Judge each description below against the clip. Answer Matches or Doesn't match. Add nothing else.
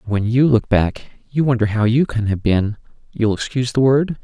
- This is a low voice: Matches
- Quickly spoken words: Matches